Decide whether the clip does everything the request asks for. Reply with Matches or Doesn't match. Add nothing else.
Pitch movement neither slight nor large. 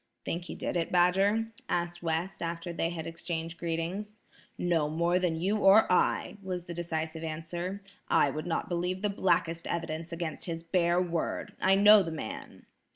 Doesn't match